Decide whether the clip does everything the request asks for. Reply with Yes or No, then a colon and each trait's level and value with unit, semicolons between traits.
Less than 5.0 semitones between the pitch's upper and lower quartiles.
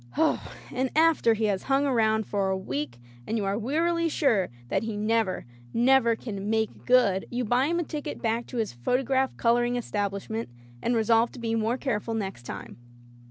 Yes: average, 3.6 semitones